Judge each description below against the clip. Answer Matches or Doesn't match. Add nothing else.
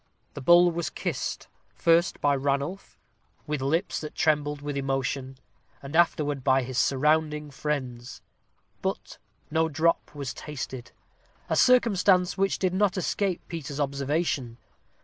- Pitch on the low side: Doesn't match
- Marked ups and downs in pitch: Doesn't match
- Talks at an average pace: Doesn't match